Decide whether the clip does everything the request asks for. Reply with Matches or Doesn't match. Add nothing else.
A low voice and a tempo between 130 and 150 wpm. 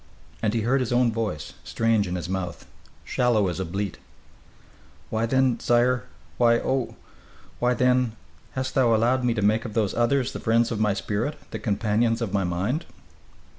Doesn't match